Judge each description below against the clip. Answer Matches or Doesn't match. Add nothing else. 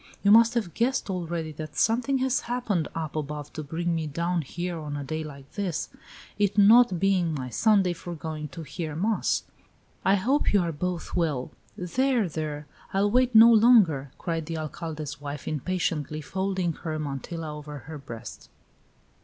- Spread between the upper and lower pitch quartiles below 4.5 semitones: Doesn't match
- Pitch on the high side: Doesn't match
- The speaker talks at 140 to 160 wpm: Doesn't match